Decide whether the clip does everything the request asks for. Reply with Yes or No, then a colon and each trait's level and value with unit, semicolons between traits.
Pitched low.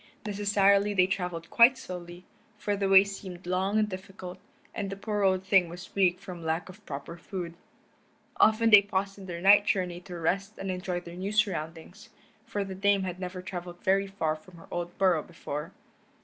No: high, 190 Hz